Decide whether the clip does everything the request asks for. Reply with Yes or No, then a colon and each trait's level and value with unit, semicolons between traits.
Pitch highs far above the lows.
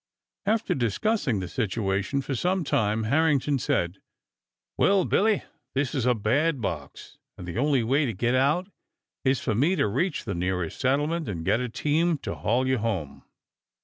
Yes: wide, 6.2 semitones